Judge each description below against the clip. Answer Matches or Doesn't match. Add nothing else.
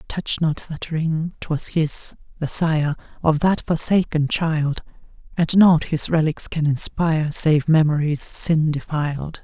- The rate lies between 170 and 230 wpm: Doesn't match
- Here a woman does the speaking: Matches